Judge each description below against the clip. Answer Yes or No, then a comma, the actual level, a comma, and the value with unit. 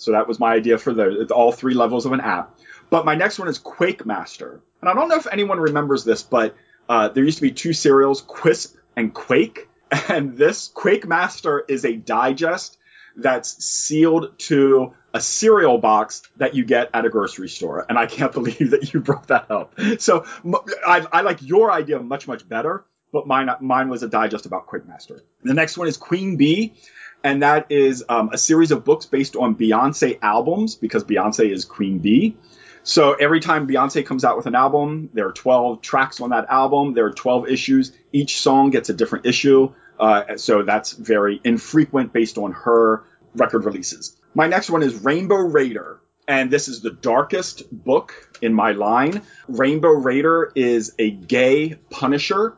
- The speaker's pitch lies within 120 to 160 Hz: Yes, medium, 140 Hz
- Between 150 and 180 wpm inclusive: No, average, 190 wpm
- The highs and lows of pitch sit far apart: No, average, 5.0 semitones